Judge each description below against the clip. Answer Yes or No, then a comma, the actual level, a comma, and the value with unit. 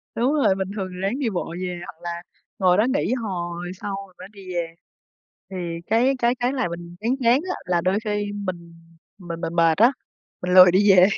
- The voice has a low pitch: No, high, 190 Hz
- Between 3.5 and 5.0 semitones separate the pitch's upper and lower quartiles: Yes, average, 4.3 semitones